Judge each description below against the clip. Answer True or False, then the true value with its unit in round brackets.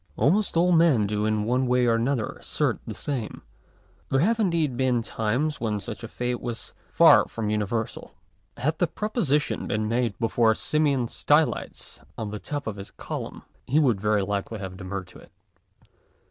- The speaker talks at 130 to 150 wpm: False (175 wpm)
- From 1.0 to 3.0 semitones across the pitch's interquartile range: False (5.4 semitones)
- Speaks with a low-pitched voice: True (120 Hz)